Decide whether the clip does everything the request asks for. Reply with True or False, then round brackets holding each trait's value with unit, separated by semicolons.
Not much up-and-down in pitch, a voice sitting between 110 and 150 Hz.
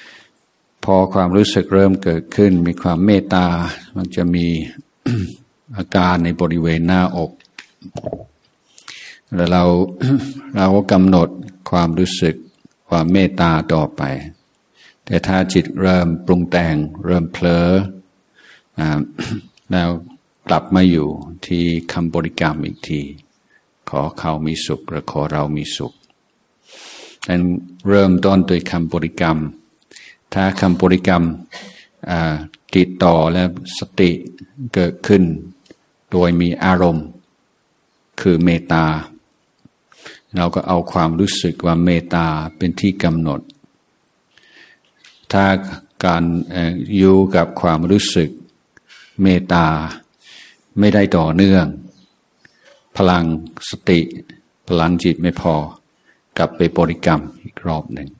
False (2.1 semitones; 90 Hz)